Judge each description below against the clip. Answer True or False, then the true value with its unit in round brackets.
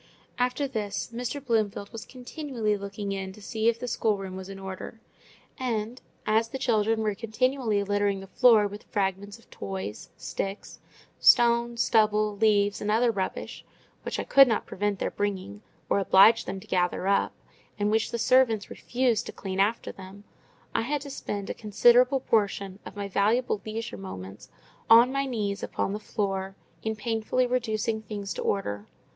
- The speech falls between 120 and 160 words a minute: False (170 wpm)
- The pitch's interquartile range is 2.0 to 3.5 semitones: True (2.9 semitones)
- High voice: True (215 Hz)